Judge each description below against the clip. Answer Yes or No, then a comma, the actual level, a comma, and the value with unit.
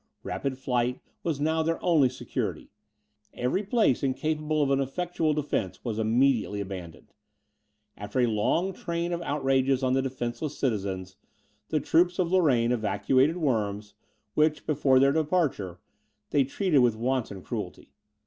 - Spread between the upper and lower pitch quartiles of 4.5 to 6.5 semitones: Yes, average, 4.9 semitones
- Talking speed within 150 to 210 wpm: No, average, 140 wpm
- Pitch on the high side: No, low, 135 Hz